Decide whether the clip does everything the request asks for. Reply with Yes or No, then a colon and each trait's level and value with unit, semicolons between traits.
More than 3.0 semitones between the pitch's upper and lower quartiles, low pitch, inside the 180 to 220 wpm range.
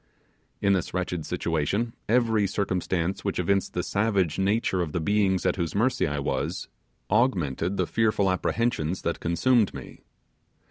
No: average, 3.6 semitones; very low, 95 Hz; average, 145 wpm